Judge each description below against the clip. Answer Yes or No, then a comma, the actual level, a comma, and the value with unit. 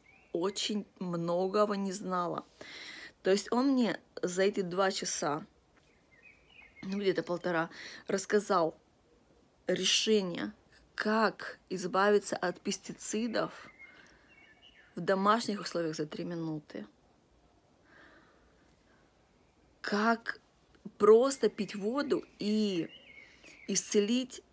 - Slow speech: Yes, slow, 80 wpm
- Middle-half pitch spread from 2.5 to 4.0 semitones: Yes, average, 3.0 semitones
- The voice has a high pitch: Yes, high, 200 Hz